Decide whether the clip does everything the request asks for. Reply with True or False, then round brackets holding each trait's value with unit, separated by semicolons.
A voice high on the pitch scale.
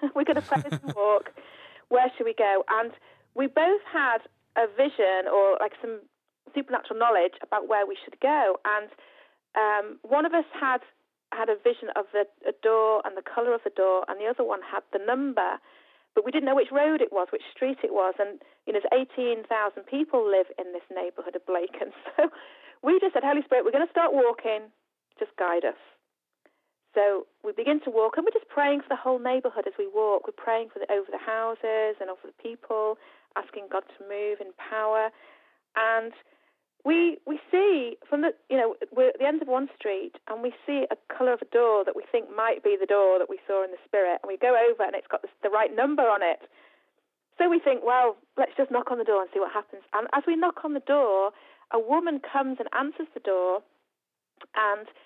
True (240 Hz)